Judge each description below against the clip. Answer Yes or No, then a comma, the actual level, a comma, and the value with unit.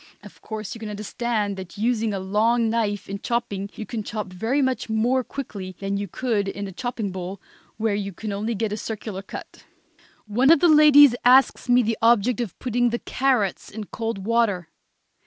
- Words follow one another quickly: No, average, 190 wpm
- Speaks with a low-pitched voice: No, high, 220 Hz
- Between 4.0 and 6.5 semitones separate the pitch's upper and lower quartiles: No, average, 3.1 semitones